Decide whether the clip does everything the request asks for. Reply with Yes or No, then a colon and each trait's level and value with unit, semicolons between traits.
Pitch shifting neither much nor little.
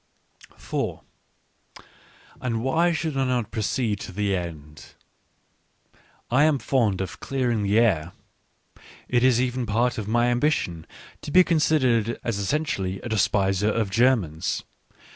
Yes: average, 4.7 semitones